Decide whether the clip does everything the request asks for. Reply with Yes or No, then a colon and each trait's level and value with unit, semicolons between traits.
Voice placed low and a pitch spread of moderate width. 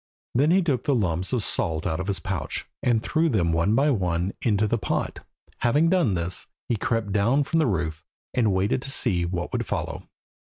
No: low, 105 Hz; wide, 6.6 semitones